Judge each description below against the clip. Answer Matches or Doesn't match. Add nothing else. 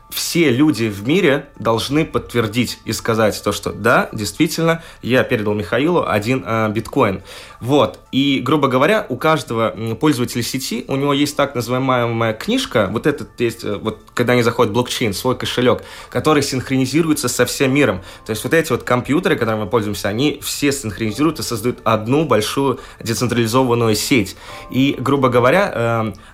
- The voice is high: Doesn't match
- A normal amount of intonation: Matches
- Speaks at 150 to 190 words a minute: Matches